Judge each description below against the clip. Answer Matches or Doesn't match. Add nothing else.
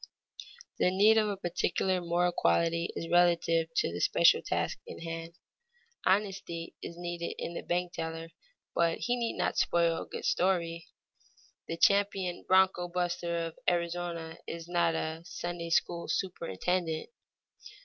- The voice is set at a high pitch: Doesn't match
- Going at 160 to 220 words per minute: Doesn't match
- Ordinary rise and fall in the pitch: Doesn't match